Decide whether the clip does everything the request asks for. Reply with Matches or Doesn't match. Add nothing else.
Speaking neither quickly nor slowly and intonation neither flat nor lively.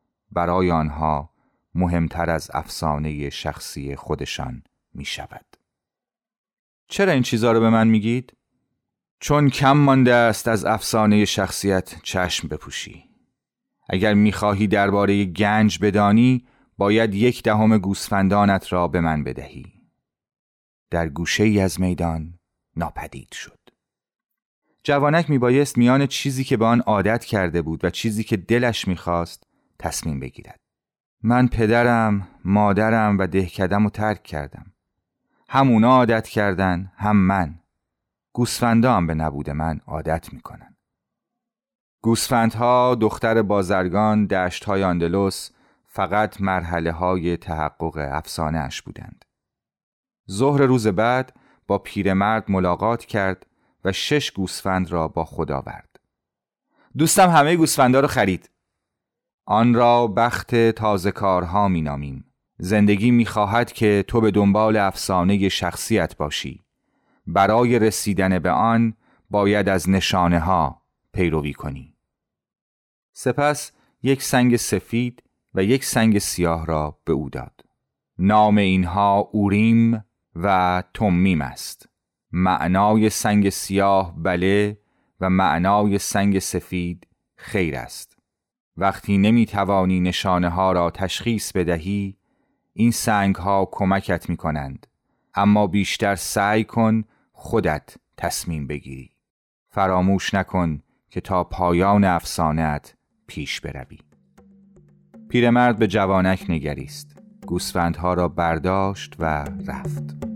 Matches